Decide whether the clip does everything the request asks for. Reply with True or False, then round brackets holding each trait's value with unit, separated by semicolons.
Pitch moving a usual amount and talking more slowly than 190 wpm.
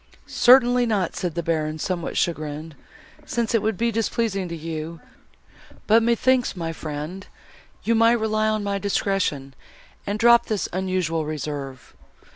False (5.8 semitones; 140 wpm)